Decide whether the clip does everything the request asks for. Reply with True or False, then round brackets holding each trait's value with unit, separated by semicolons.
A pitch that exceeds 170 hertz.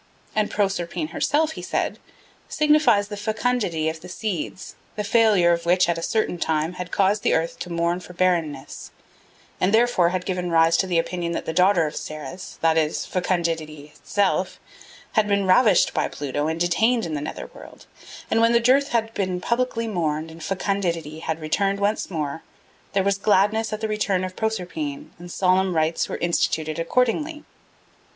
True (185 Hz)